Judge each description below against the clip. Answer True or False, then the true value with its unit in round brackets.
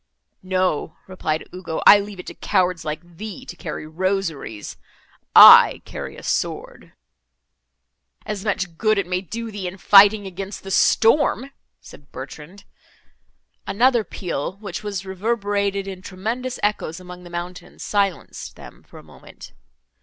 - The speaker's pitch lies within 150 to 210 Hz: True (190 Hz)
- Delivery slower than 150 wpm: True (140 wpm)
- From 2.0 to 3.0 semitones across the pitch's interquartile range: True (2.7 semitones)